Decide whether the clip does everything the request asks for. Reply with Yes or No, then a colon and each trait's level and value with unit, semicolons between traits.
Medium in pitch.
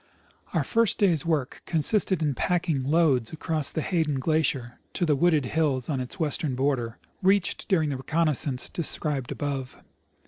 Yes: medium, 150 Hz